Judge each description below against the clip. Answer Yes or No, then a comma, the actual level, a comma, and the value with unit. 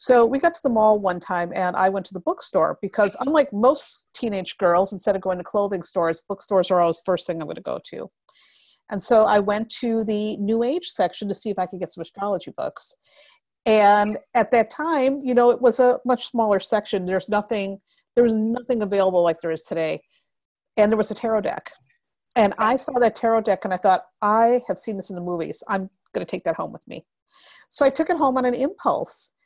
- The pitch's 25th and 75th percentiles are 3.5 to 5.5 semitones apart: Yes, average, 4.3 semitones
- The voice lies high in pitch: Yes, high, 210 Hz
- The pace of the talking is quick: Yes, fast, 230 wpm